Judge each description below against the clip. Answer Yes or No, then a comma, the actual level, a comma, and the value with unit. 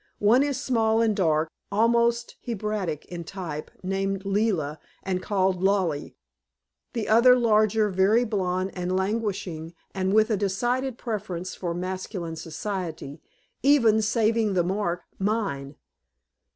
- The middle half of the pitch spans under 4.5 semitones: Yes, average, 3.6 semitones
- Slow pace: Yes, slow, 125 wpm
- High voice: Yes, high, 195 Hz